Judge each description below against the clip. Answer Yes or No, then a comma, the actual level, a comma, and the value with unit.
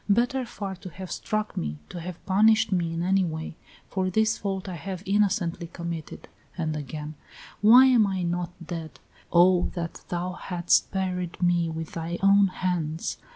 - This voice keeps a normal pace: Yes, average, 165 wpm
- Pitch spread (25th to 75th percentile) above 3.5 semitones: No, average, 2.7 semitones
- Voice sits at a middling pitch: Yes, medium, 180 Hz